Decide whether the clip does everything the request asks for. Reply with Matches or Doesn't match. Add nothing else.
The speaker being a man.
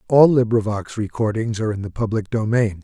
Matches